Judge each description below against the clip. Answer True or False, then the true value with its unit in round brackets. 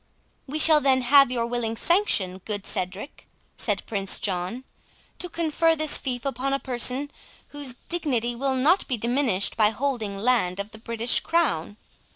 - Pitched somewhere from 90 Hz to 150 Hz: False (245 Hz)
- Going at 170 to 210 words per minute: False (160 wpm)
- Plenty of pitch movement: False (4.7 semitones)